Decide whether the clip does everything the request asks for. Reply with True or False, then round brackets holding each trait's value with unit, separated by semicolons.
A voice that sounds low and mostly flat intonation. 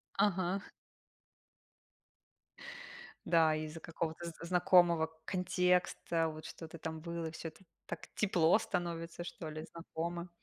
False (170 Hz; 1.7 semitones)